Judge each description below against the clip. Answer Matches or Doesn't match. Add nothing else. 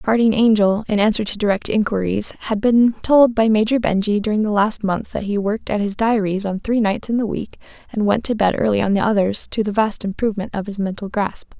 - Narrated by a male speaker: Doesn't match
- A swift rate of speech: Matches